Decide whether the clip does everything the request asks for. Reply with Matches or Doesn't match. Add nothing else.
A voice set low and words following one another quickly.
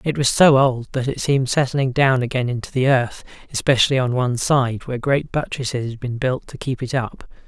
Matches